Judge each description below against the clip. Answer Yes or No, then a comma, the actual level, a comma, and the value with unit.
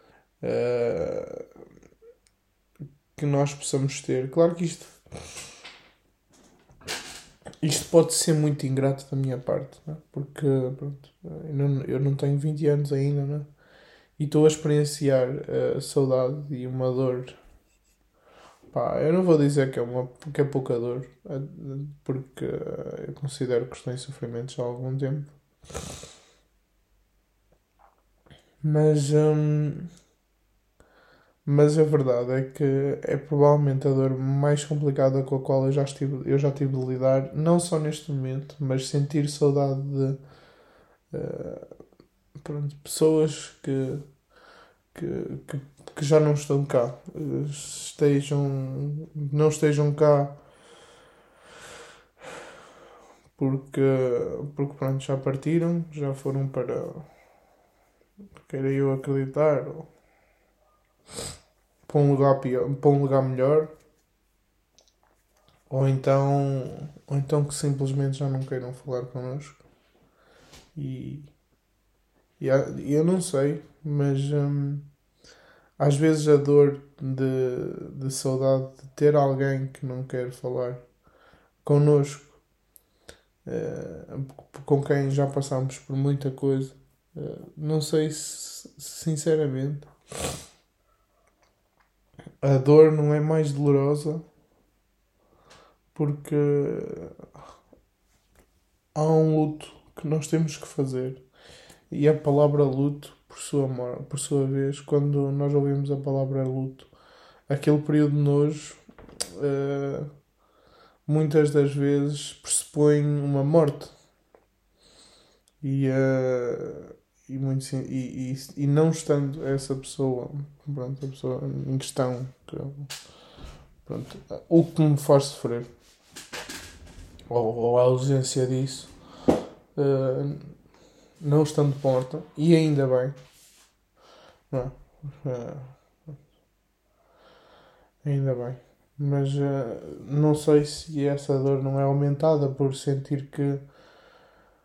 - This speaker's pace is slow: Yes, slow, 105 wpm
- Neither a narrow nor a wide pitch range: No, narrow, 2.0 semitones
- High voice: No, medium, 140 Hz